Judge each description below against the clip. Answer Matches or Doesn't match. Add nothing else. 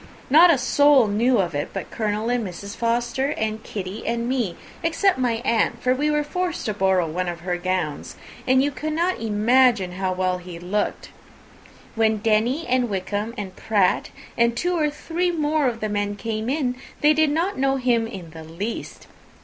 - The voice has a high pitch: Matches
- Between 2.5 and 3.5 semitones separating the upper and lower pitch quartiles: Doesn't match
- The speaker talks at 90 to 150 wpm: Doesn't match